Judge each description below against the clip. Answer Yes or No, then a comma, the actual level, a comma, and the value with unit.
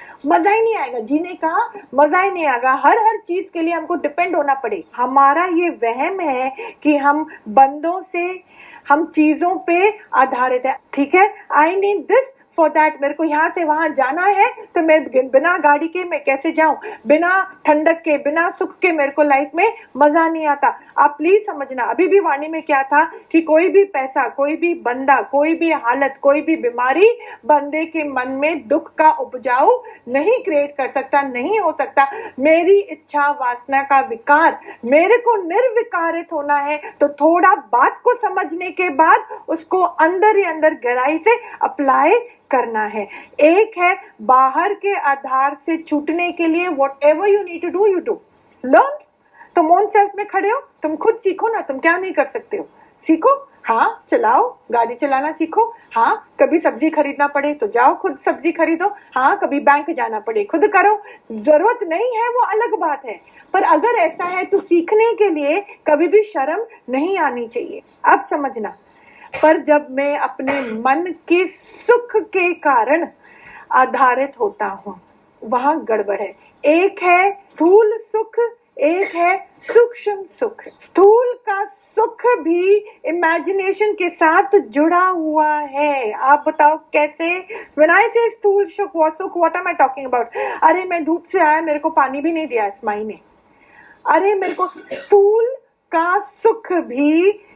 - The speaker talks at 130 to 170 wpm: Yes, average, 165 wpm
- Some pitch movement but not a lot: No, wide, 5.8 semitones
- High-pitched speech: Yes, very high, 335 Hz